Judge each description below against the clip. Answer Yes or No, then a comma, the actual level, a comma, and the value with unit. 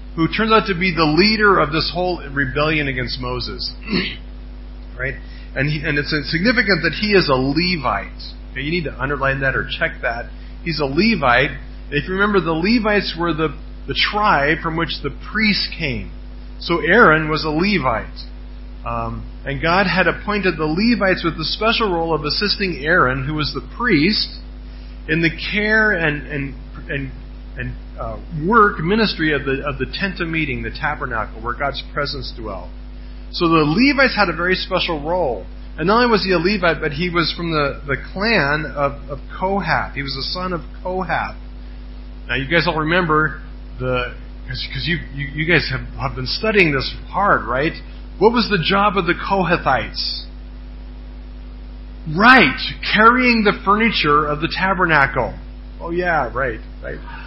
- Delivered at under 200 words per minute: Yes, average, 170 wpm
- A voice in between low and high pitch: Yes, medium, 155 Hz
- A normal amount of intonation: No, wide, 6.0 semitones